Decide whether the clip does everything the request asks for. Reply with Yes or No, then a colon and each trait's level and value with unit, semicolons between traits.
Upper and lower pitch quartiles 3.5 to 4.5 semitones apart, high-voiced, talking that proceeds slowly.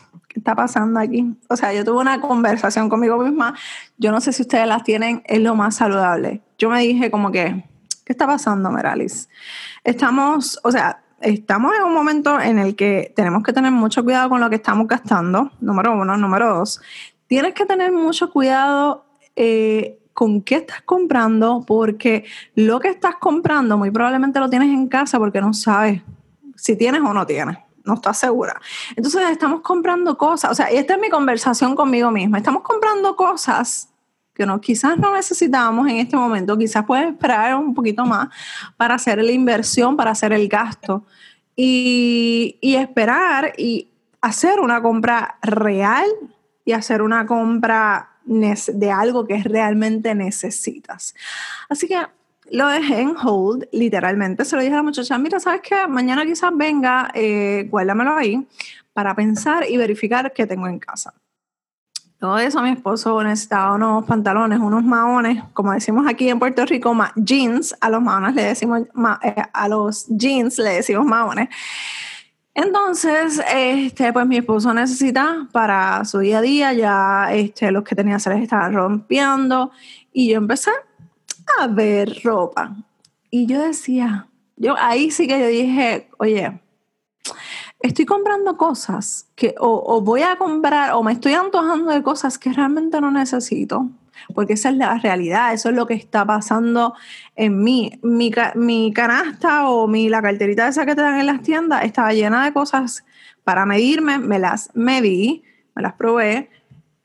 No: average, 4.2 semitones; high, 235 Hz; average, 165 wpm